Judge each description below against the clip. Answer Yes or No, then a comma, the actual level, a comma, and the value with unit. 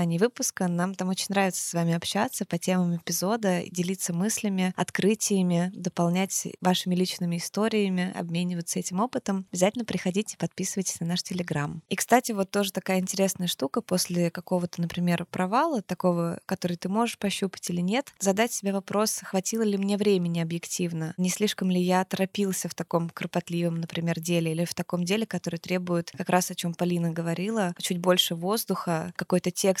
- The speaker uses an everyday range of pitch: No, narrow, 2.1 semitones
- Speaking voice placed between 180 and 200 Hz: Yes, medium, 185 Hz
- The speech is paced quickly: Yes, fast, 165 wpm